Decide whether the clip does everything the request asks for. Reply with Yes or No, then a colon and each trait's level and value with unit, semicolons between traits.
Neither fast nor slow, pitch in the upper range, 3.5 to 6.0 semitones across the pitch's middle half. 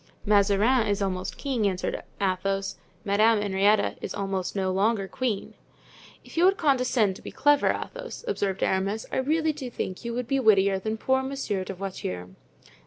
Yes: average, 170 wpm; high, 205 Hz; average, 4.9 semitones